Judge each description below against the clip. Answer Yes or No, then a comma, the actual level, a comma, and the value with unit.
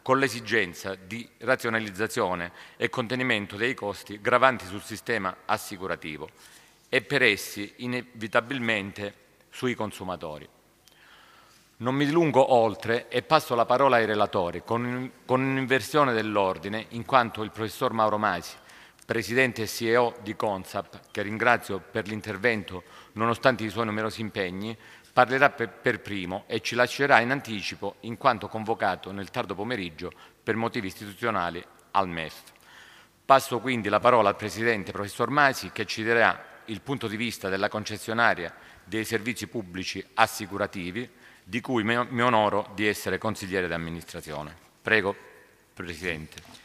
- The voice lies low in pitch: Yes, low, 110 Hz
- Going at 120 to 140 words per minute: Yes, average, 130 wpm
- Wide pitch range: No, average, 3.3 semitones